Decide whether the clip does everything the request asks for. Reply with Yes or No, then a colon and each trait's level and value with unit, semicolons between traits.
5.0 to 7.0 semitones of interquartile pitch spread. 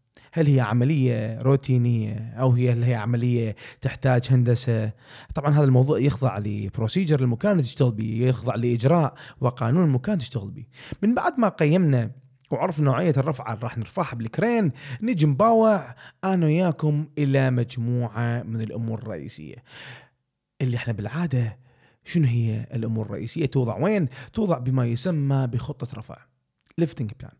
No: average, 4.2 semitones